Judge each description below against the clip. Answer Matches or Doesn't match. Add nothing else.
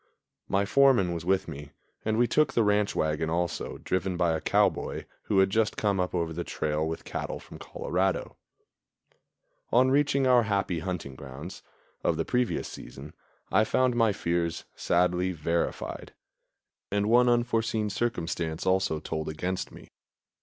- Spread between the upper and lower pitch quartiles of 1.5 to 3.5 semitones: Doesn't match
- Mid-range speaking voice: Doesn't match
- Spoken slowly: Doesn't match